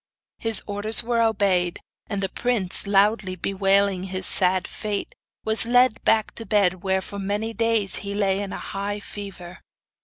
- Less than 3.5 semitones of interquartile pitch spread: Yes, narrow, 2.4 semitones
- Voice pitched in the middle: No, high, 200 Hz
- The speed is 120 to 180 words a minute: Yes, average, 160 wpm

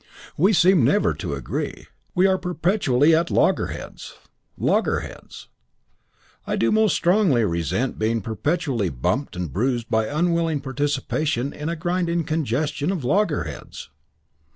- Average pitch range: No, wide, 6.7 semitones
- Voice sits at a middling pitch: Yes, medium, 150 Hz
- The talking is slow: Yes, slow, 125 wpm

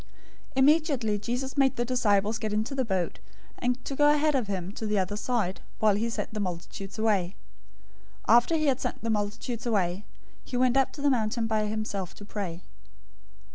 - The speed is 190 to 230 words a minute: Yes, average, 195 wpm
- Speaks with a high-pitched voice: Yes, high, 220 Hz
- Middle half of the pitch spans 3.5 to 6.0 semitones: Yes, average, 3.8 semitones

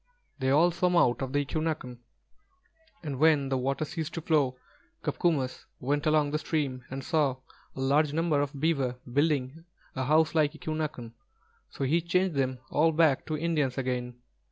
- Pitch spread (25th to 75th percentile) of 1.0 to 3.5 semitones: Yes, average, 3.1 semitones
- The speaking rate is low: No, average, 165 wpm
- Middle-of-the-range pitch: Yes, medium, 145 Hz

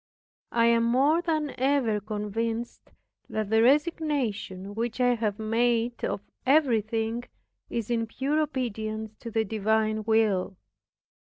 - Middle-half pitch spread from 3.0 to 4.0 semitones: No, narrow, 2.6 semitones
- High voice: Yes, high, 230 Hz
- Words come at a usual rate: No, slow, 120 wpm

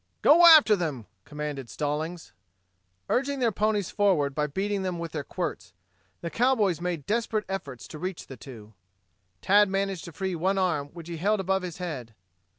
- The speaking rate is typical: Yes, average, 170 wpm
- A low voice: No, medium, 180 Hz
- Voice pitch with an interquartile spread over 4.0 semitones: Yes, average, 5.3 semitones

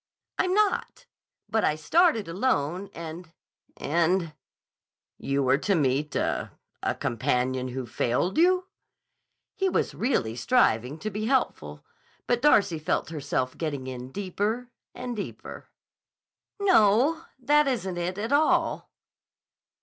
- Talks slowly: Yes, slow, 115 wpm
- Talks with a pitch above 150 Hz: Yes, medium, 185 Hz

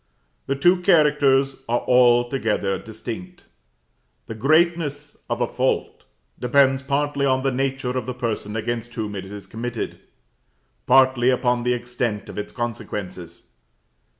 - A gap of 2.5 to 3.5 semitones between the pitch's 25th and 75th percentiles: Yes, average, 3.1 semitones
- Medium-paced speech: No, slow, 130 wpm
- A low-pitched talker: Yes, low, 125 Hz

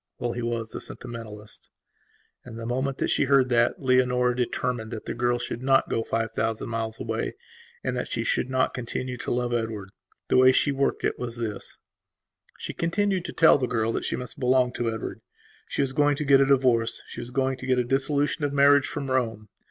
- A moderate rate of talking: No, fast, 215 wpm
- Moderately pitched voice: No, low, 125 Hz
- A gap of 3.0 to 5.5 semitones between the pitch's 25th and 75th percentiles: No, narrow, 2.6 semitones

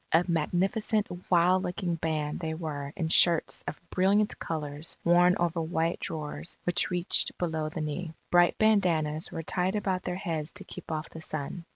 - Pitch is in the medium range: Yes, medium, 170 Hz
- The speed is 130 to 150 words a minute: No, average, 170 wpm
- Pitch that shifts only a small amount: Yes, narrow, 2.3 semitones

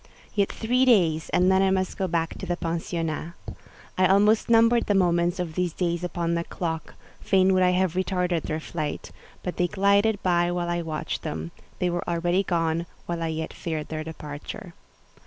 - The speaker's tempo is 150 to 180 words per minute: No, average, 190 wpm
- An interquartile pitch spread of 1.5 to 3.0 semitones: Yes, narrow, 2.4 semitones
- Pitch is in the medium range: Yes, medium, 175 Hz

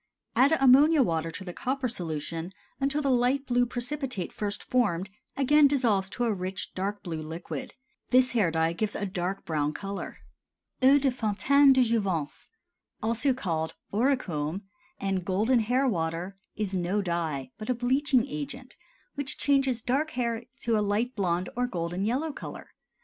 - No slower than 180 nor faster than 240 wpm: No, average, 160 wpm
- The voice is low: No, high, 215 Hz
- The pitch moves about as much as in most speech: No, wide, 6.4 semitones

